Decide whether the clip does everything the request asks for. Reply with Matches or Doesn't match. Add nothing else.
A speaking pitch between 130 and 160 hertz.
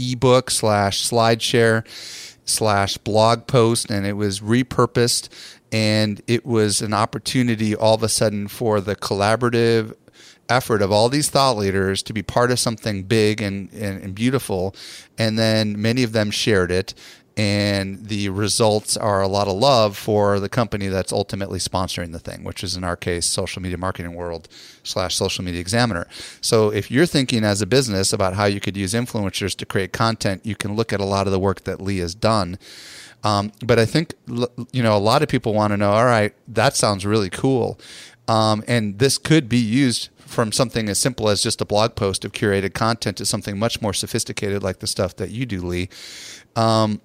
Doesn't match